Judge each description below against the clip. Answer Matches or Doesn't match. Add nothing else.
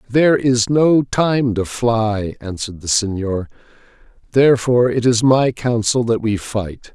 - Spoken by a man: Matches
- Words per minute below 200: Matches